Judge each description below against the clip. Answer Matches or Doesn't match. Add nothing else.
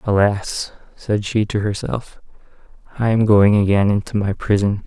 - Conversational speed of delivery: Matches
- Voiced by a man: Matches